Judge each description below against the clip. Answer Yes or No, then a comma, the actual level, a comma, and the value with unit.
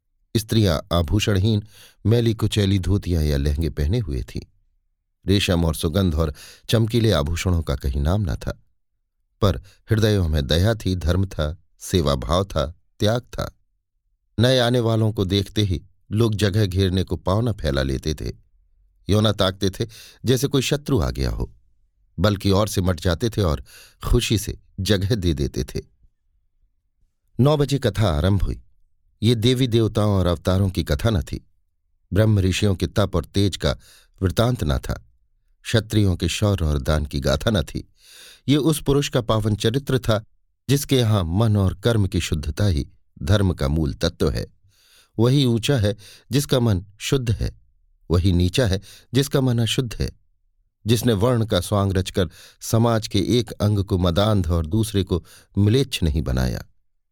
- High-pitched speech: No, low, 100 Hz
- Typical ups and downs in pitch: Yes, average, 4.5 semitones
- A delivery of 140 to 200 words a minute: Yes, average, 165 wpm